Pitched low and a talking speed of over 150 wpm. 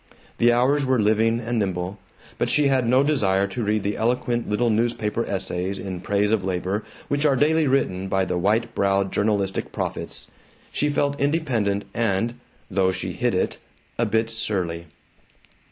Yes: low, 110 Hz; average, 165 wpm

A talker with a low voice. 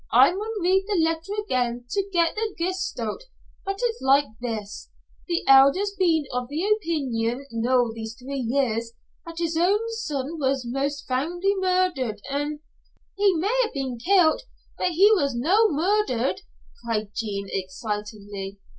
No: very high, 290 Hz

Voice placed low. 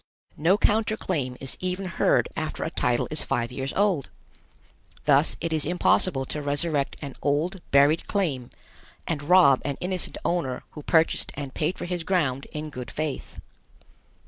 No: medium, 150 Hz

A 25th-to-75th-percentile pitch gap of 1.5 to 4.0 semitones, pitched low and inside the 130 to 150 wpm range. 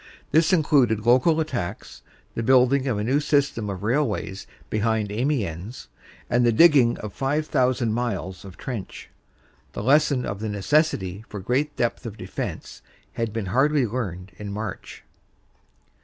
No: average, 5.0 semitones; low, 120 Hz; average, 145 wpm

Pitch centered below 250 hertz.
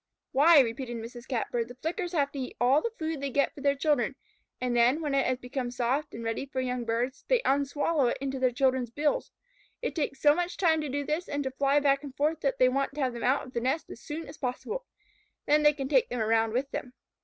No: very high, 275 Hz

